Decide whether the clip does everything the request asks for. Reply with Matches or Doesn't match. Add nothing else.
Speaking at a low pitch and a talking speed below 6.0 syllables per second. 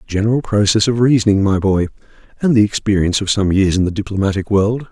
Doesn't match